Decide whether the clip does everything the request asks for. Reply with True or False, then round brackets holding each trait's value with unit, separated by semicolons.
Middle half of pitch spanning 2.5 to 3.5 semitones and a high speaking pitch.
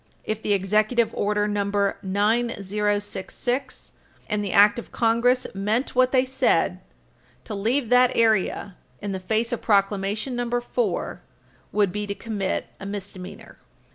True (3.0 semitones; 210 Hz)